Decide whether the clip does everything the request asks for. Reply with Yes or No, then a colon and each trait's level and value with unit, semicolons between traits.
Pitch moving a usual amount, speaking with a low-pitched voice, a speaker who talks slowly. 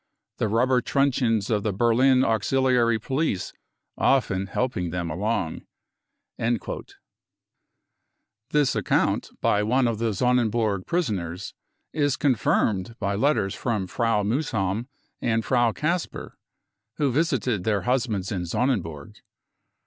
Yes: average, 4.6 semitones; low, 115 Hz; slow, 105 wpm